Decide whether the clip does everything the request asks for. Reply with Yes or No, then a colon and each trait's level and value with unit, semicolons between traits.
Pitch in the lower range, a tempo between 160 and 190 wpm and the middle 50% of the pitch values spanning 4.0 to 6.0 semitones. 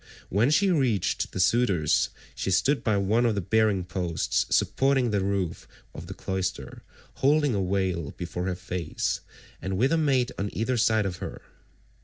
Yes: low, 100 Hz; average, 170 wpm; average, 5.0 semitones